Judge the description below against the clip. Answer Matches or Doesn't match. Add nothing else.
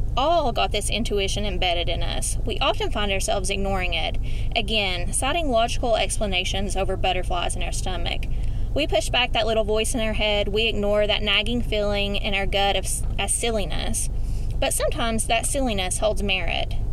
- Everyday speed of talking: Matches